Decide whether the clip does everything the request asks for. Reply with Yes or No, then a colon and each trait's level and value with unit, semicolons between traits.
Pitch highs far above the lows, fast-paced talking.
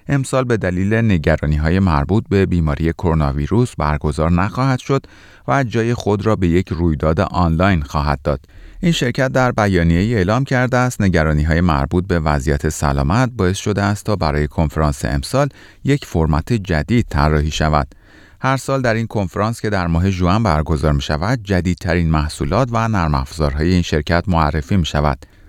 Yes: wide, 5.9 semitones; fast, 165 wpm